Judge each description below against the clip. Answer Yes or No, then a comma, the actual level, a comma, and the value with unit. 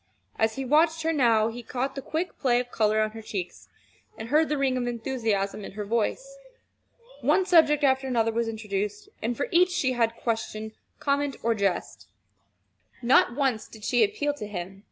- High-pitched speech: Yes, high, 240 Hz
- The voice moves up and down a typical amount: Yes, average, 4.6 semitones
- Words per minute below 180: No, average, 185 wpm